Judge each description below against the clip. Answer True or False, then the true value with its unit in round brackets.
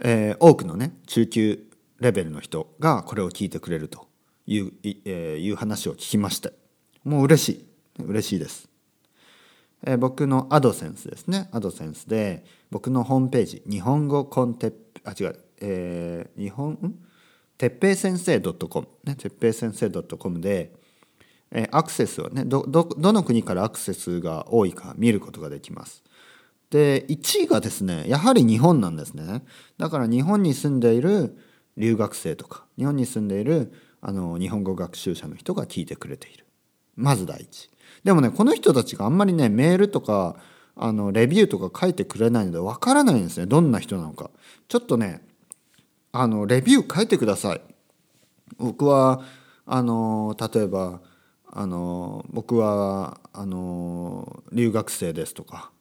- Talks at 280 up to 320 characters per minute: True (315 characters per minute)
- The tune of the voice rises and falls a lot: True (6.6 semitones)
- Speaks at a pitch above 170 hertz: False (115 Hz)